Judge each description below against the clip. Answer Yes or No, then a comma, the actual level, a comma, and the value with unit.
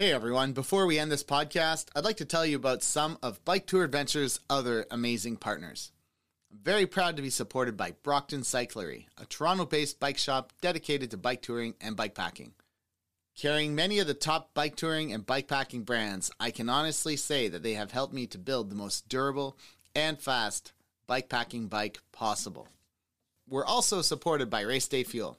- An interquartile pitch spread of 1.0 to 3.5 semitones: No, average, 4.5 semitones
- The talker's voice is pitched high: No, low, 135 Hz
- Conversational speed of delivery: Yes, average, 190 wpm